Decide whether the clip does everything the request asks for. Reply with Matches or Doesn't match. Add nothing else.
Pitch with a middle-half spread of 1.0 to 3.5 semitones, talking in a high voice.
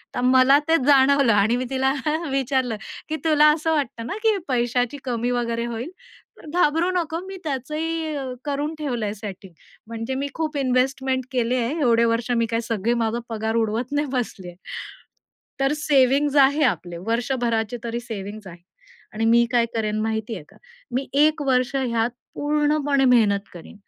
Doesn't match